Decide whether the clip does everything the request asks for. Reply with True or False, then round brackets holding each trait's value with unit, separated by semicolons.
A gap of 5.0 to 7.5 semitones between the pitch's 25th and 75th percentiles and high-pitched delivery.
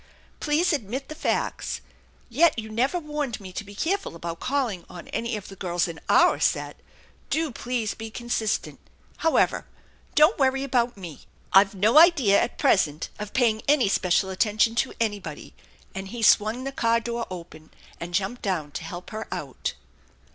True (5.5 semitones; 220 Hz)